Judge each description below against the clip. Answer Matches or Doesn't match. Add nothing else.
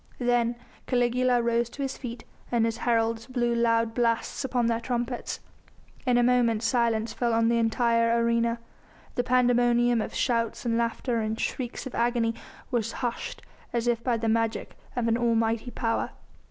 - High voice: Matches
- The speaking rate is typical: Matches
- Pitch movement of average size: Doesn't match